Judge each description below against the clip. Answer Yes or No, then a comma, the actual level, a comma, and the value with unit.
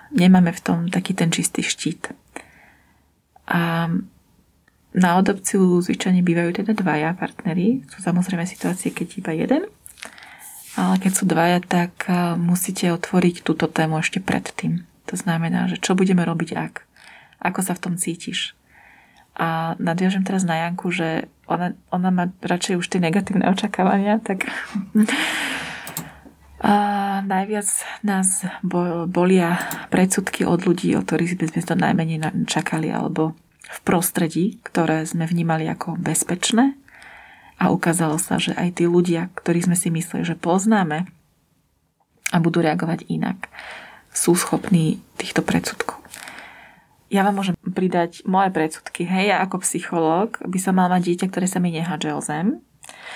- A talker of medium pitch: Yes, medium, 180 Hz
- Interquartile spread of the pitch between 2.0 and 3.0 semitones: Yes, narrow, 2.4 semitones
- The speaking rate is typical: Yes, average, 140 wpm